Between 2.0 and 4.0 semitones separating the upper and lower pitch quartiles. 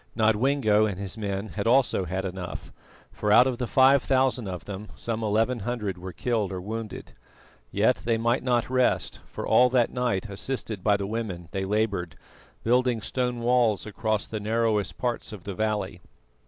Yes: average, 3.4 semitones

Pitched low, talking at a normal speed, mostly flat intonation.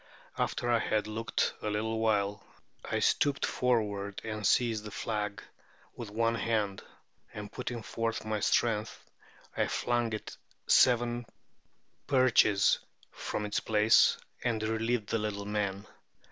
No: low, 110 Hz; slow, 130 wpm; narrow, 1.8 semitones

